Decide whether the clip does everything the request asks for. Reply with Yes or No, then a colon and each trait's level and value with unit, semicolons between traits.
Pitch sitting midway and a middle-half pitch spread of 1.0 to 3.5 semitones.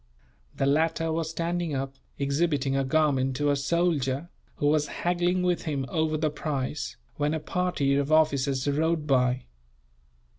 Yes: medium, 150 Hz; average, 2.9 semitones